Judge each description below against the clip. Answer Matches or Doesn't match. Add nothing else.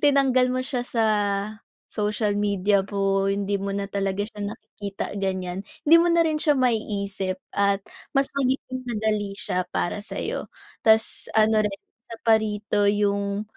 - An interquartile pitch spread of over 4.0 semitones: Doesn't match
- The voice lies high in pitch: Matches